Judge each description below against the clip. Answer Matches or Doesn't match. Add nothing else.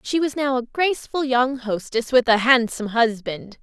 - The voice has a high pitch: Matches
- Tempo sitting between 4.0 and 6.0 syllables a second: Matches